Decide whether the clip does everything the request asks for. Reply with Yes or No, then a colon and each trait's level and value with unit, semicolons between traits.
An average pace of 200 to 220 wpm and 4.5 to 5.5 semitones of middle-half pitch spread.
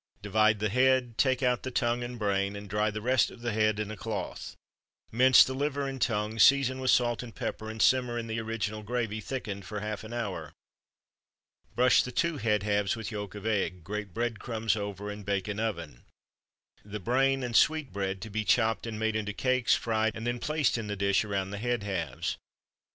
No: fast, 205 wpm; average, 2.9 semitones